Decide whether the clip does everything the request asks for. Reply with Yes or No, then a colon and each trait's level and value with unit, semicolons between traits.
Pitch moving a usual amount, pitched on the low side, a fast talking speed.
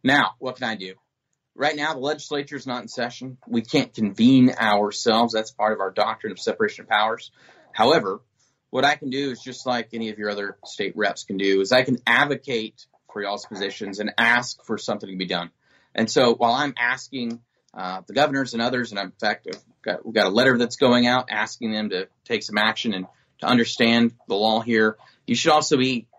Yes: average, 3.5 semitones; low, 120 Hz; fast, 220 wpm